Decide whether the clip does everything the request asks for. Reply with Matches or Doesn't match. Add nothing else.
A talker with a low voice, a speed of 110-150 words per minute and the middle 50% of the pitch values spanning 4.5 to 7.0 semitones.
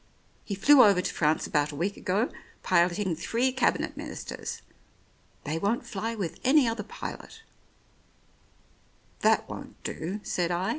Doesn't match